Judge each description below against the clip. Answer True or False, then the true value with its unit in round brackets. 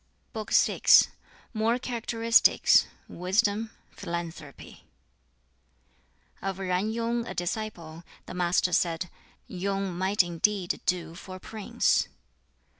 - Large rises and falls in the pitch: False (3.7 semitones)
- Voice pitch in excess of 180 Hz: True (190 Hz)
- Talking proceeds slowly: True (105 wpm)